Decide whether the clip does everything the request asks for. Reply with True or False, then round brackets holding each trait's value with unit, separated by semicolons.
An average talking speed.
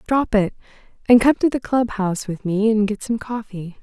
False (220 wpm)